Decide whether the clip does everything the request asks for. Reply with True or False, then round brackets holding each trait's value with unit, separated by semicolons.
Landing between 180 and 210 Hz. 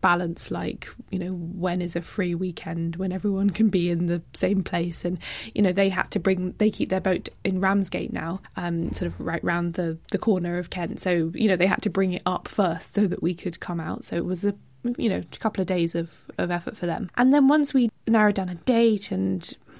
True (185 Hz)